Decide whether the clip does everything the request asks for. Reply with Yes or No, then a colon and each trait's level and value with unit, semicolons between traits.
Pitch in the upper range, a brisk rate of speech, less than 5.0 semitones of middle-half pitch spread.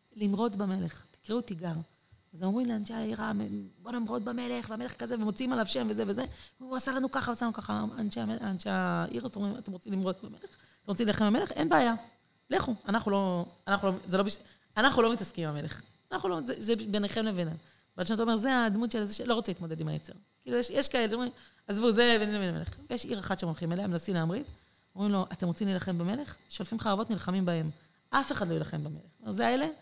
Yes: high, 205 Hz; fast, 165 wpm; average, 4.3 semitones